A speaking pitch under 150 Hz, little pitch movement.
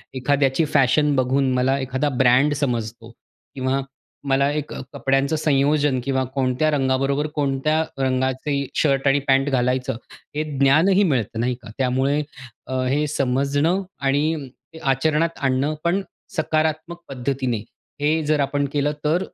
Yes: medium, 140 Hz; narrow, 2.3 semitones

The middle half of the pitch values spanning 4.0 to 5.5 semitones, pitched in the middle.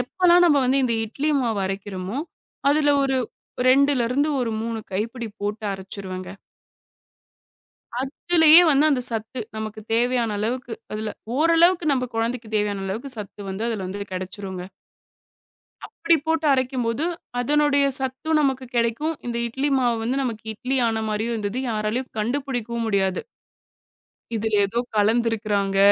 No: average, 4.3 semitones; high, 235 Hz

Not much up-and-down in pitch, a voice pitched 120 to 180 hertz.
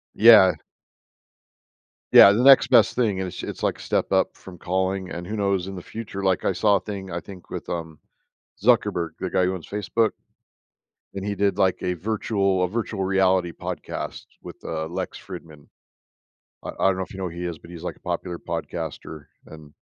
No: narrow, 2.3 semitones; very low, 95 Hz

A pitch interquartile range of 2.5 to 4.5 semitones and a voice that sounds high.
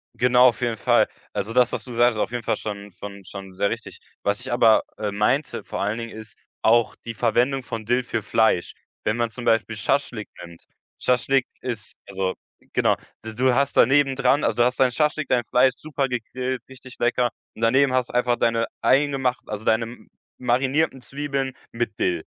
No: average, 2.8 semitones; low, 120 Hz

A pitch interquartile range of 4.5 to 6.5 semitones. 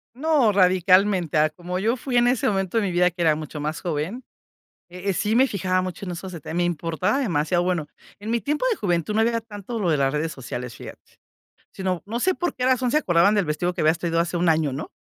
Yes: average, 4.8 semitones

